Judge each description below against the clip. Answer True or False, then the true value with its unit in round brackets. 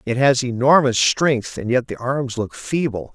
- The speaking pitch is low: True (125 Hz)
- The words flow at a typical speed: True (190 wpm)